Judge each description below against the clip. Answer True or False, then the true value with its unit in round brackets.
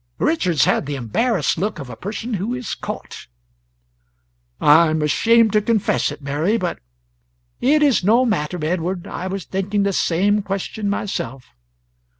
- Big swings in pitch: True (5.7 semitones)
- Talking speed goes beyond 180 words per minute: False (155 wpm)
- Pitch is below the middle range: False (190 Hz)